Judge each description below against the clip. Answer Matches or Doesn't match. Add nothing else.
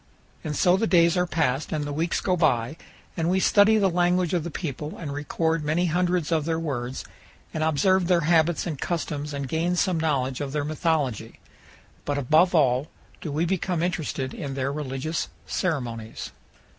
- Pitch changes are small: Doesn't match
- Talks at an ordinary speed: Matches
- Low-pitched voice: Doesn't match